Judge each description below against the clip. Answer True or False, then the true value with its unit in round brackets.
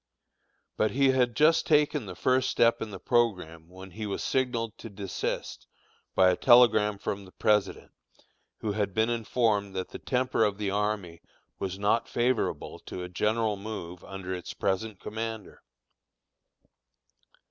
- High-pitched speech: False (105 Hz)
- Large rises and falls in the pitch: False (3.5 semitones)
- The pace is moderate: True (150 wpm)